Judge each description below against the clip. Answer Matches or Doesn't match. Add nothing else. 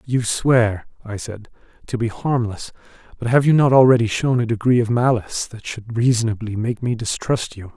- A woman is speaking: Doesn't match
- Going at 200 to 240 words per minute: Doesn't match